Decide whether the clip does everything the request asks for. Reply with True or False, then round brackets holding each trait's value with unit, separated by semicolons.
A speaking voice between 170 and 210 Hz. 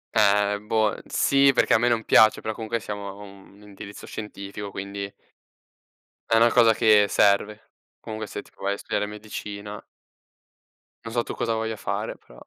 False (105 Hz)